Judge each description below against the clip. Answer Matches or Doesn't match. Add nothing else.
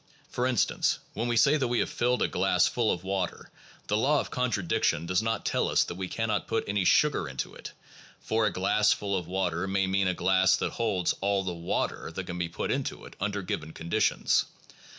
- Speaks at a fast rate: Matches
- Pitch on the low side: Matches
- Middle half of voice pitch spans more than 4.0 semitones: Doesn't match